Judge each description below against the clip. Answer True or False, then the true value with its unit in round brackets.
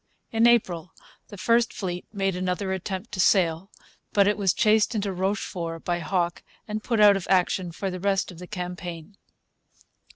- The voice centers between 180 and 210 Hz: True (190 Hz)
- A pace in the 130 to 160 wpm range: False (170 wpm)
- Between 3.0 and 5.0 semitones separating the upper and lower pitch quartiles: False (2.6 semitones)